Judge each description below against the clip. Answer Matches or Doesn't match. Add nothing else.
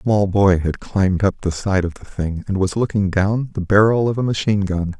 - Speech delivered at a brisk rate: Matches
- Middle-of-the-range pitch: Doesn't match